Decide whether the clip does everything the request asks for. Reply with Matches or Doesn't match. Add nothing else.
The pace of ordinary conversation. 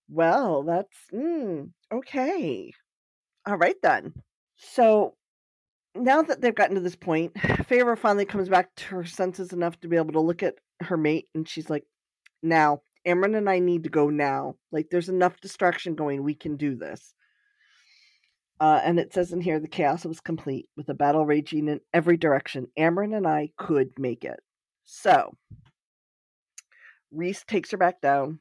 Matches